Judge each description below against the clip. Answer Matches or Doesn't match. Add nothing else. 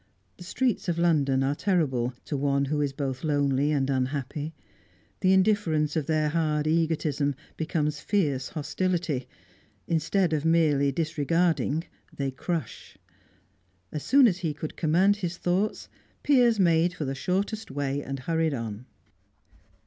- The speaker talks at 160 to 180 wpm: Doesn't match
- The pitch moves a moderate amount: Matches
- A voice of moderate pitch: Matches